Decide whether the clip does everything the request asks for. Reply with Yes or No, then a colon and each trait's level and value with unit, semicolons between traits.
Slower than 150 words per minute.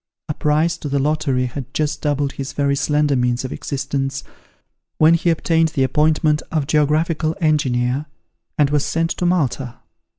No: average, 160 wpm